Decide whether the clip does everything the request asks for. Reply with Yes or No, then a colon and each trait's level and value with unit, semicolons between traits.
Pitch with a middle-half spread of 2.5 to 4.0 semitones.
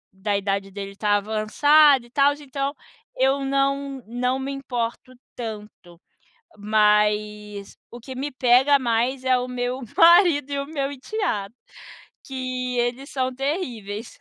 No: average, 4.5 semitones